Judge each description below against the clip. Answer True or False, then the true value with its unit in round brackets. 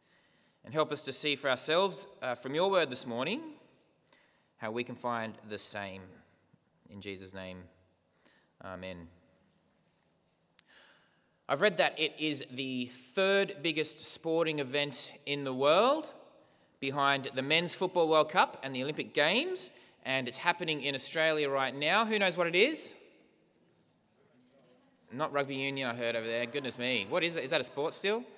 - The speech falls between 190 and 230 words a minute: False (160 wpm)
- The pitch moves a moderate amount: False (5.9 semitones)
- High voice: False (140 Hz)